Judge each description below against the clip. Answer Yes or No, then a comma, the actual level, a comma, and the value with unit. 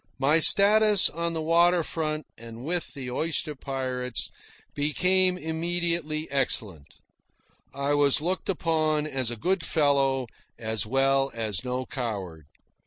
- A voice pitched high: No, medium, 145 Hz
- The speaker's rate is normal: No, slow, 125 wpm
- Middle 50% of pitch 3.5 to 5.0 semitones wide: Yes, average, 4.6 semitones